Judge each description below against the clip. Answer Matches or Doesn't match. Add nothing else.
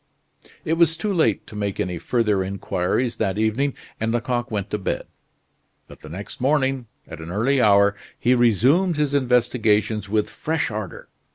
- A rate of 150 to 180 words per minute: Matches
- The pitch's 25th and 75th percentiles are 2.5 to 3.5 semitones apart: Doesn't match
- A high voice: Doesn't match